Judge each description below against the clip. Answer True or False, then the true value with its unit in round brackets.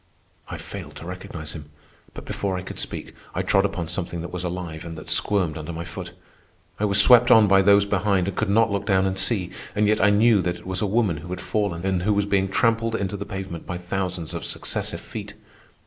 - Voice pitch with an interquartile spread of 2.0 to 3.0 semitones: True (2.5 semitones)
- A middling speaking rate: False (235 wpm)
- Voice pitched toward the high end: False (95 Hz)